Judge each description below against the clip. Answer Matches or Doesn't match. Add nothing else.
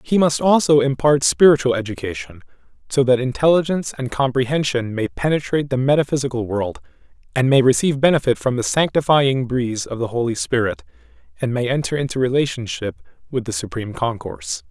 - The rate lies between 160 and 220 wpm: Doesn't match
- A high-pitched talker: Doesn't match